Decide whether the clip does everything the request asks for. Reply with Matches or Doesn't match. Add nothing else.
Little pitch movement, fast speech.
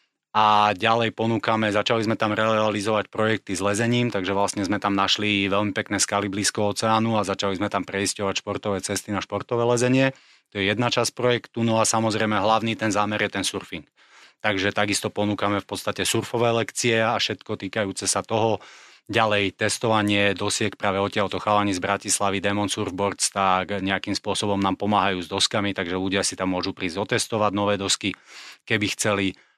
Matches